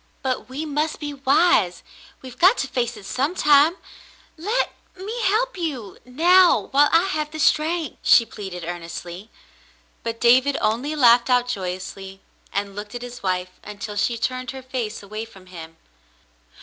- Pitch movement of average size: No, wide, 6.7 semitones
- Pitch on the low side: No, very high, 250 Hz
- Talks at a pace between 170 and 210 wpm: No, average, 160 wpm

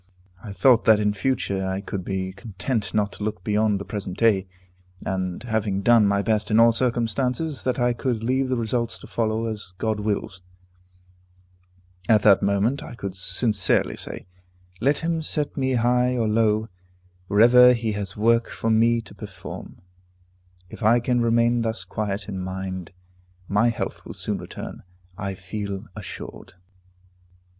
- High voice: No, low, 110 Hz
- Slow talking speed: No, average, 160 wpm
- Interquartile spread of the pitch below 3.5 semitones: Yes, average, 3.1 semitones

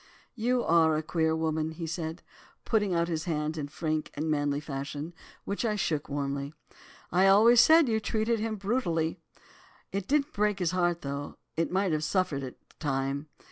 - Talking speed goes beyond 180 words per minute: No, average, 175 wpm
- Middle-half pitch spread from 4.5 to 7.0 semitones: Yes, average, 4.9 semitones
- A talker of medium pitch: Yes, medium, 165 Hz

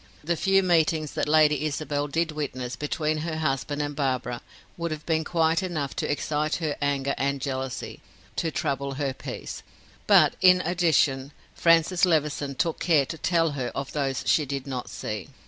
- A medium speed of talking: Yes, average, 170 wpm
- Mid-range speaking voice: Yes, medium, 150 Hz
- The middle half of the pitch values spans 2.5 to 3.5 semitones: Yes, average, 2.9 semitones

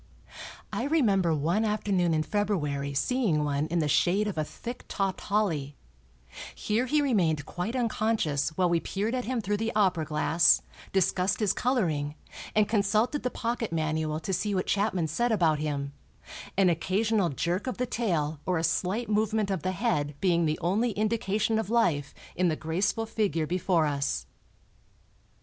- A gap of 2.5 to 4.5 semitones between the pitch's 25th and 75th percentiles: No, wide, 5.5 semitones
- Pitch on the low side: No, high, 190 Hz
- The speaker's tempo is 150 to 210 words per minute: Yes, average, 165 wpm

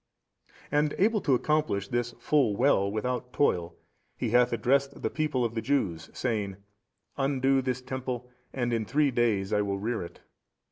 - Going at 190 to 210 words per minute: No, average, 160 wpm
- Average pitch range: Yes, average, 4.1 semitones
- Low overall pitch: Yes, low, 125 Hz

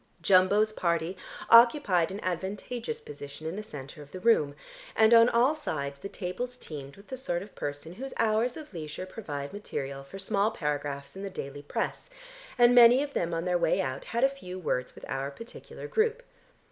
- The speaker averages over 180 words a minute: Yes, average, 190 wpm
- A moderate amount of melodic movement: No, wide, 7.8 semitones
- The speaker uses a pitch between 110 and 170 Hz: No, medium, 185 Hz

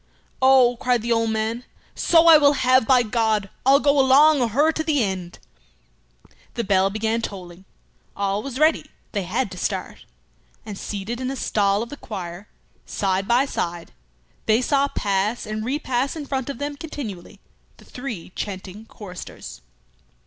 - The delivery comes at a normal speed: Yes, average, 165 wpm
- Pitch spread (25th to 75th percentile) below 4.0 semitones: No, average, 5.2 semitones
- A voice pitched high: Yes, high, 230 Hz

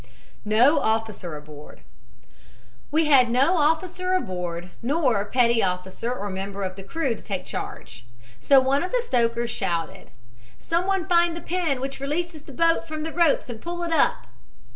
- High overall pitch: Yes, very high, 260 Hz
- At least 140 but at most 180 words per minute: Yes, average, 165 wpm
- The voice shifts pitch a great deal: Yes, wide, 8.6 semitones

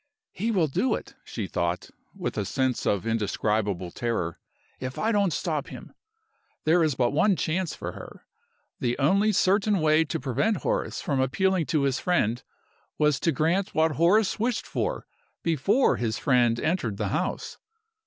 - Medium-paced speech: Yes, average, 165 wpm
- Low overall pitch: No, medium, 150 Hz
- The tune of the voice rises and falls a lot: Yes, wide, 7.7 semitones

